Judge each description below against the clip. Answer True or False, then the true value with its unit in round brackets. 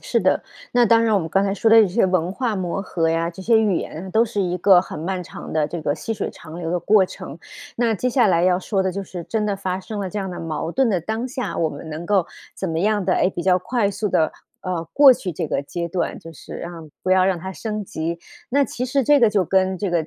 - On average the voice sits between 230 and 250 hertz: False (190 Hz)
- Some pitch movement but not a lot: True (4.1 semitones)